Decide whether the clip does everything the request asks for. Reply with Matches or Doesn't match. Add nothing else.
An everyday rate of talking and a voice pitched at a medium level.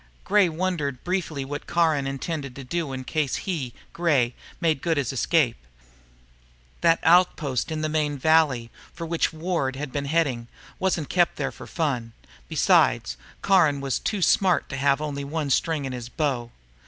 Matches